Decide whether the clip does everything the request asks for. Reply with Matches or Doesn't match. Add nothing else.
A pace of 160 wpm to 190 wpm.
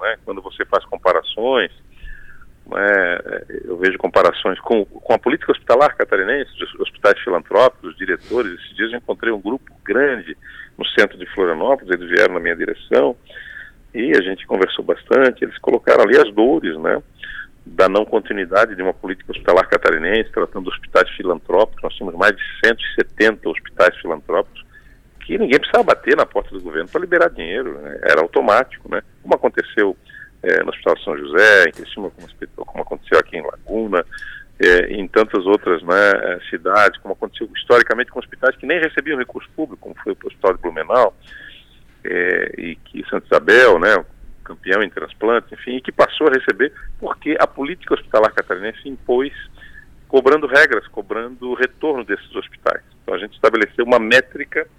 Matches